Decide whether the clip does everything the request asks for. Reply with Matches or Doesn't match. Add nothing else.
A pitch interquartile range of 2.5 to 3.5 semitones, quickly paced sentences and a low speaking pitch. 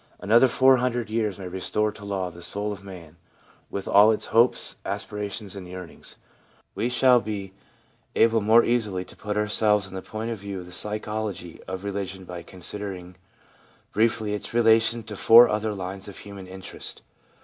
Doesn't match